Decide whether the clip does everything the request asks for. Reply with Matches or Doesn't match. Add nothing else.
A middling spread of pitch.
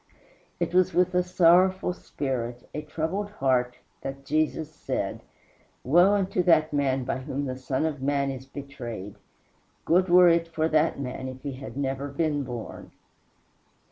Matches